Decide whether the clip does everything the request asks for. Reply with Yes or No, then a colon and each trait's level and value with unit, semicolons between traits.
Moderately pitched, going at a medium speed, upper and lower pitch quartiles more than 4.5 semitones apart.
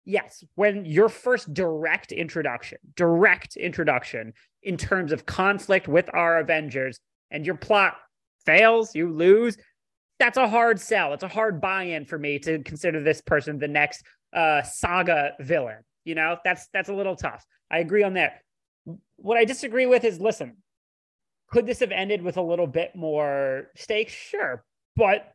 Yes: medium, 175 Hz; average, 165 wpm; average, 5.1 semitones